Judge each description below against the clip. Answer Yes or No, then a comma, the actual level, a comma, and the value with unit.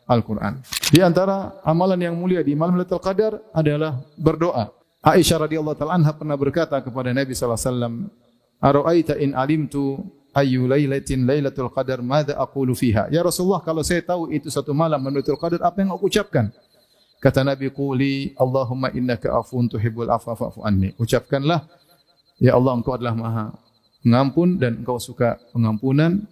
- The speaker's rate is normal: No, fast, 150 wpm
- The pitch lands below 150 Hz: Yes, medium, 140 Hz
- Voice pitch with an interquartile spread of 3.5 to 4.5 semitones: No, average, 5.0 semitones